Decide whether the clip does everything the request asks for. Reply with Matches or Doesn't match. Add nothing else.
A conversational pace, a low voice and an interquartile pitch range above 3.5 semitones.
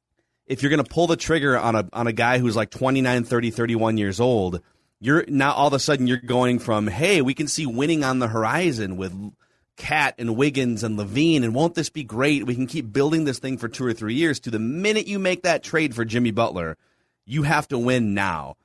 Doesn't match